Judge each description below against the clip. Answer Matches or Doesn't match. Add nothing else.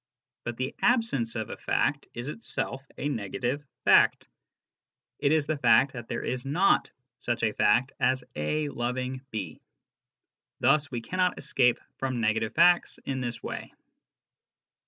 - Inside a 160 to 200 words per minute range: Doesn't match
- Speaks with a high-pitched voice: Doesn't match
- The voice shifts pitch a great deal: Doesn't match